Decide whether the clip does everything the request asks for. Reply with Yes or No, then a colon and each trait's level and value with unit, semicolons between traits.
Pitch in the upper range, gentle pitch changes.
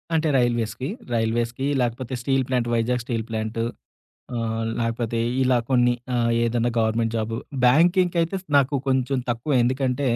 No: low, 120 Hz; narrow, 2.3 semitones